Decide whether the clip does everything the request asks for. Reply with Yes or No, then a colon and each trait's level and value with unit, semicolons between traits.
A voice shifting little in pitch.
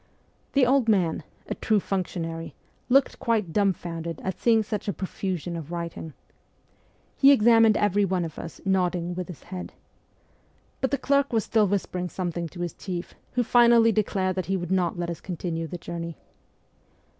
No: average, 4.1 semitones